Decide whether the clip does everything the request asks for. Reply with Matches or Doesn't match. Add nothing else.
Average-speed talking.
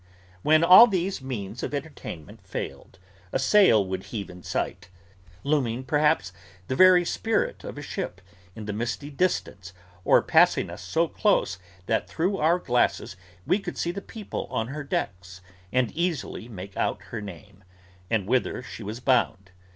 Matches